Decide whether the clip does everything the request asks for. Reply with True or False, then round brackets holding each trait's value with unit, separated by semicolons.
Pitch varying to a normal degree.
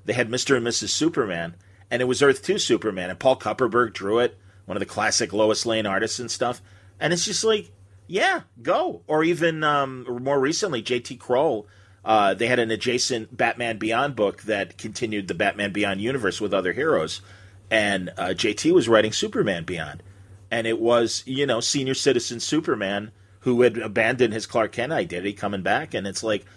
True (4.1 semitones)